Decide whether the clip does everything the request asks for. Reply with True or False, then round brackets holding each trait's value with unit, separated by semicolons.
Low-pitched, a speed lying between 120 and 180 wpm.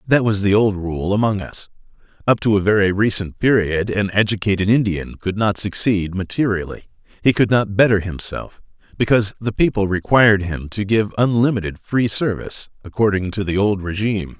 True (100 Hz; 165 wpm)